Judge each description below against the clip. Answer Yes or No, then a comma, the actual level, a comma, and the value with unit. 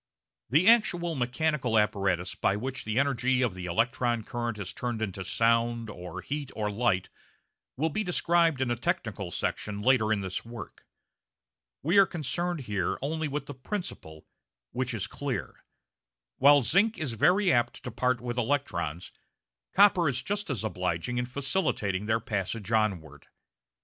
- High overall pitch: No, low, 120 Hz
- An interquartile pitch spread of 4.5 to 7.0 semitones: Yes, wide, 5.5 semitones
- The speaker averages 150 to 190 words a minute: Yes, average, 155 wpm